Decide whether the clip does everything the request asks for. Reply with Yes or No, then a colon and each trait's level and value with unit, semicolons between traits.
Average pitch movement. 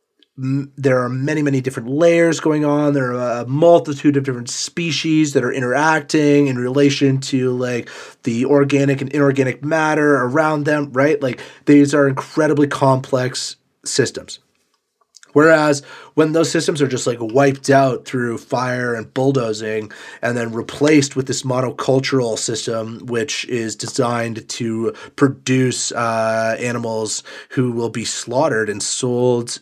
Yes: average, 3.0 semitones